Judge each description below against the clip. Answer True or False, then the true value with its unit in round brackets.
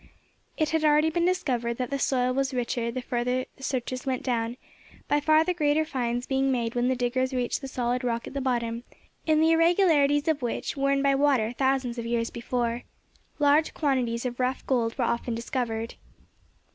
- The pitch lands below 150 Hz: False (255 Hz)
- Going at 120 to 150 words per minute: False (190 wpm)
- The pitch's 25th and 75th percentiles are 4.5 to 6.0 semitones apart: False (3.2 semitones)